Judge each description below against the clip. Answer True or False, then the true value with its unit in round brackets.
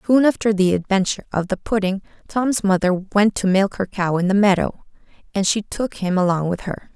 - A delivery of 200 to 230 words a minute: True (205 wpm)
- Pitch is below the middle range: False (195 Hz)